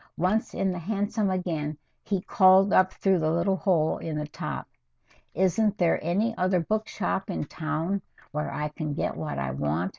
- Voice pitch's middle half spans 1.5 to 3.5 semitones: No, average, 4.0 semitones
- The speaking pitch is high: No, medium, 180 Hz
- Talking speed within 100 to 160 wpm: No, average, 180 wpm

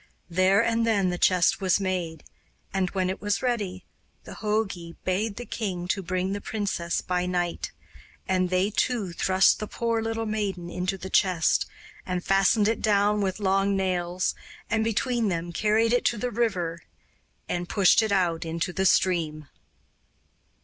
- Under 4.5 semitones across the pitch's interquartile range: Yes, average, 2.9 semitones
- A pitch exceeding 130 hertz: Yes, high, 190 Hz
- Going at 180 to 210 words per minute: No, average, 165 wpm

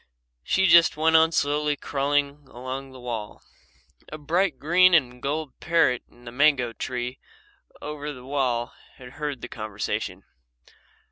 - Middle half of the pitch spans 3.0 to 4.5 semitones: Yes, average, 3.7 semitones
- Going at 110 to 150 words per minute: Yes, average, 140 wpm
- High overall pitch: No, medium, 140 Hz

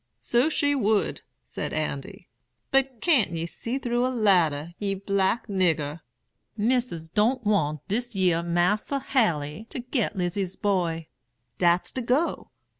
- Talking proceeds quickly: No, slow, 135 wpm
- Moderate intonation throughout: No, wide, 6.1 semitones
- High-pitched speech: Yes, high, 205 Hz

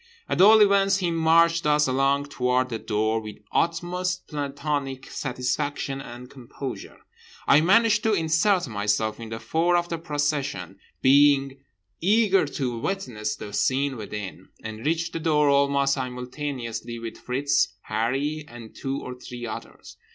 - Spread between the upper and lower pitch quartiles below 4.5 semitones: No, average, 5.3 semitones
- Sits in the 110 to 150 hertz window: Yes, medium, 140 Hz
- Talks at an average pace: Yes, average, 145 wpm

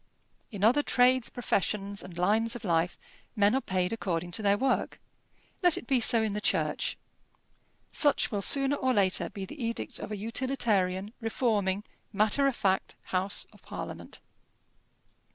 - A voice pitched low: No, high, 210 Hz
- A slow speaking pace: No, average, 155 wpm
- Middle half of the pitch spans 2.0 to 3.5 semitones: No, average, 4.3 semitones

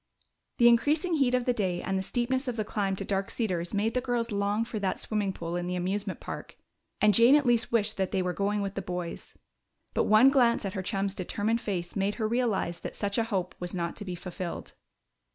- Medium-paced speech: No, fast, 230 wpm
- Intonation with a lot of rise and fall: No, average, 3.8 semitones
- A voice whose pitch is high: Yes, high, 205 Hz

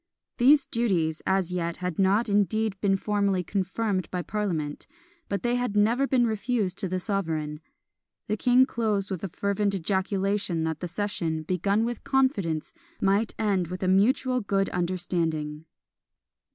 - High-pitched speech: Yes, high, 195 Hz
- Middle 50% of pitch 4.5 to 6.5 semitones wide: No, average, 3.3 semitones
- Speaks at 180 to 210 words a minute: No, average, 150 wpm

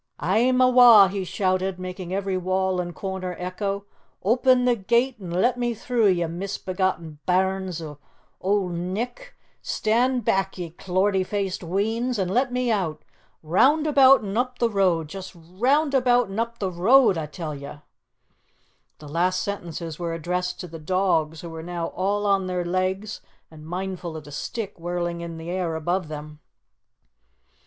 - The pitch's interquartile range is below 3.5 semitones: No, average, 3.9 semitones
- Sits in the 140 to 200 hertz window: Yes, medium, 185 Hz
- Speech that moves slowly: No, average, 165 wpm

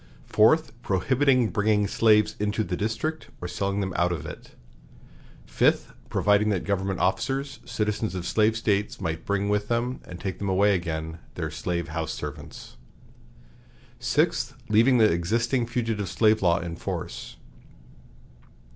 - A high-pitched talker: No, low, 105 Hz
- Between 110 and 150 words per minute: Yes, average, 140 wpm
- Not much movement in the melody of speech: No, average, 3.9 semitones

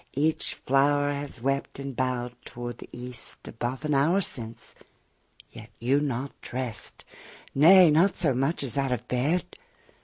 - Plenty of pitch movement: No, average, 2.9 semitones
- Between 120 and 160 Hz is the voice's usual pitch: Yes, low, 135 Hz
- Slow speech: No, average, 150 wpm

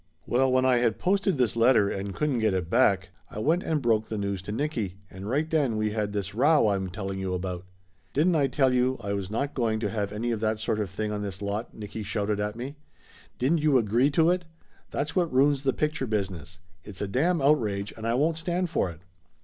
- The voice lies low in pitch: Yes, low, 115 Hz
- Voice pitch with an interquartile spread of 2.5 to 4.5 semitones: No, wide, 5.6 semitones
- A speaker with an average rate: No, fast, 235 wpm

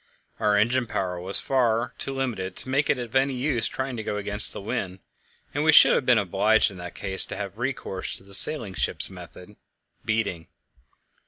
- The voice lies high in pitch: No, low, 110 Hz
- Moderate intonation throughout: Yes, average, 5.0 semitones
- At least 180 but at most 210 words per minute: Yes, average, 195 wpm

